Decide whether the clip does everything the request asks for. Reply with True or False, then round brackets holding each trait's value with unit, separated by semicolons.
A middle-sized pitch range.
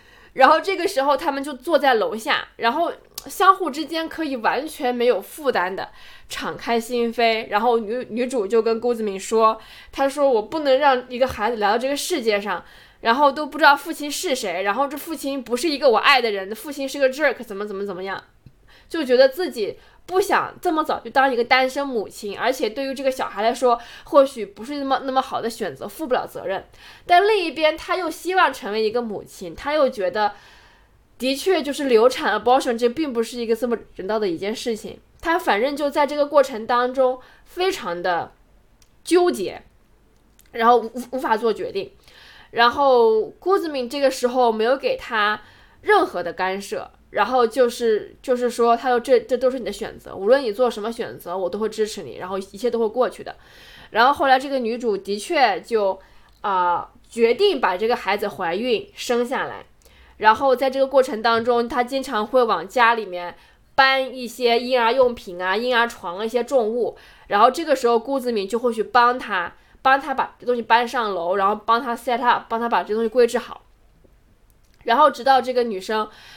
True (4.2 semitones)